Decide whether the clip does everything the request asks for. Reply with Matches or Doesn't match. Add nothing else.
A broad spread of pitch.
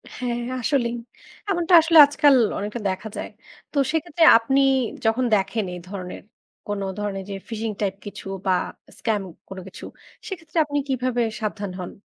Matches